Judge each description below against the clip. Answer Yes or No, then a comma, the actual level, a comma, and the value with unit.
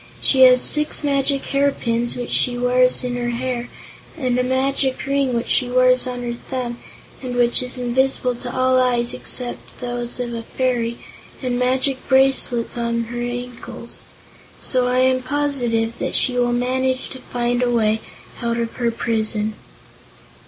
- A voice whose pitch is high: Yes, very high, 250 Hz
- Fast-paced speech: No, average, 165 wpm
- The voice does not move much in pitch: Yes, narrow, 1.4 semitones